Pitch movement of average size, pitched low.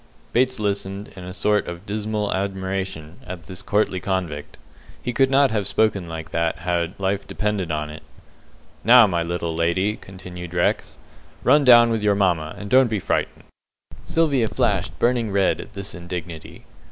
Yes: average, 3.6 semitones; very low, 95 Hz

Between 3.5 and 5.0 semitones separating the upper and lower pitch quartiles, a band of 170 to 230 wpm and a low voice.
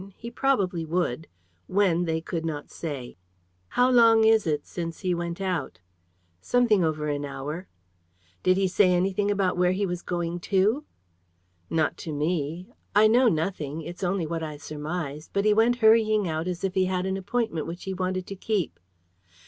No: average, 3.8 semitones; average, 180 wpm; medium, 180 Hz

